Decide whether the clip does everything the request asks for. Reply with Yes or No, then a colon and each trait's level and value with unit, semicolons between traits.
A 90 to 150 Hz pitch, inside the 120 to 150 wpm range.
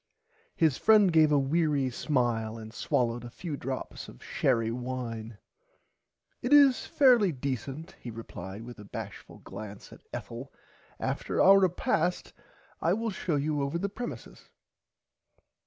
Yes: medium, 140 Hz; average, 140 wpm